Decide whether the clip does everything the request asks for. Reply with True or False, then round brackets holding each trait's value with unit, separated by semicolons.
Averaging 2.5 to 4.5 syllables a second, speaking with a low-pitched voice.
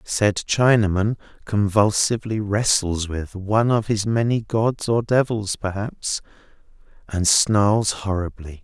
True (3.9 syllables/s; 105 Hz)